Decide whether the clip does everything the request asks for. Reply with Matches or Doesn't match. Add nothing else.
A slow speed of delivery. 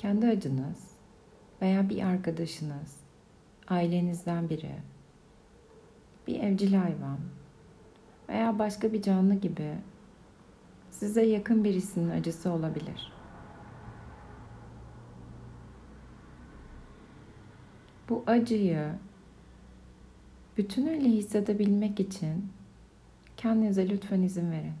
Matches